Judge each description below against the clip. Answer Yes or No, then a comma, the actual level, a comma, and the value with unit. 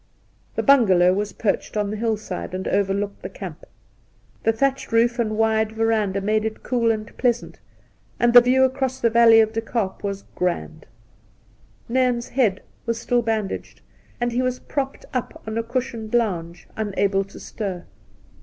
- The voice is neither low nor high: No, high, 225 Hz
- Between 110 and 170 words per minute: Yes, average, 165 wpm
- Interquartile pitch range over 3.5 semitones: No, average, 3.0 semitones